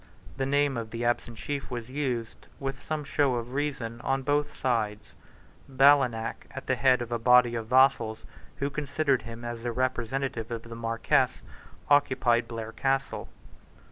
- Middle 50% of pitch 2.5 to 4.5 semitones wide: Yes, average, 2.9 semitones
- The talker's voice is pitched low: Yes, low, 125 Hz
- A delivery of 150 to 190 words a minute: Yes, average, 160 wpm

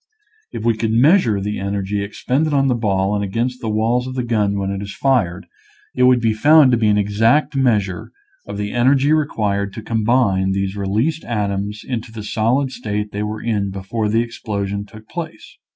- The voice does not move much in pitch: No, average, 3.7 semitones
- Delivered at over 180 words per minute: Yes, average, 200 wpm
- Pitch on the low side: Yes, low, 110 Hz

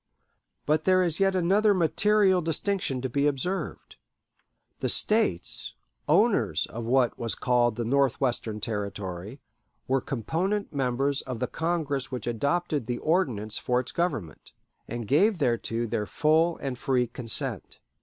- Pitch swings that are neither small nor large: No, wide, 6.3 semitones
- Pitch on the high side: No, low, 135 Hz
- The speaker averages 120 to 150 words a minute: Yes, slow, 135 wpm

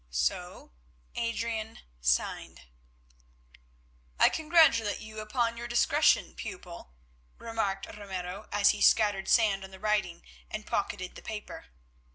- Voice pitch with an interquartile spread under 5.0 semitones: Yes, average, 2.9 semitones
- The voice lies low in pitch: No, high, 215 Hz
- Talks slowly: Yes, slow, 115 wpm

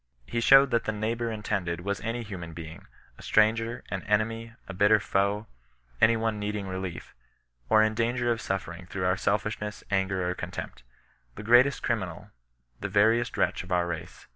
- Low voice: Yes, low, 105 Hz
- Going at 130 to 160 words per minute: No, average, 185 wpm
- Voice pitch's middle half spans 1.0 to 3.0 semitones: No, average, 3.7 semitones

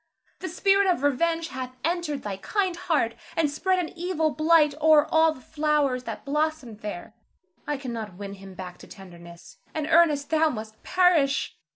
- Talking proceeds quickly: No, average, 170 wpm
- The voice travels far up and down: Yes, wide, 6.3 semitones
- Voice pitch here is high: Yes, very high, 295 Hz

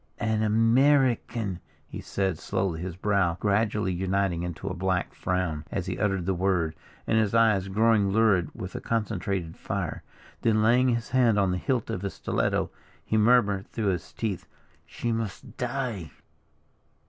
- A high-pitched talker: No, low, 100 Hz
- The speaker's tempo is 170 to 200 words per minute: No, average, 160 wpm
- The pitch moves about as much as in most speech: Yes, average, 3.5 semitones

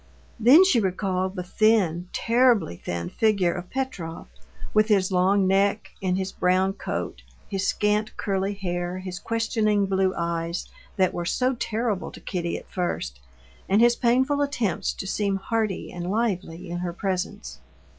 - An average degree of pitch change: Yes, average, 3.4 semitones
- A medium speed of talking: Yes, average, 155 wpm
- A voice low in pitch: No, high, 195 Hz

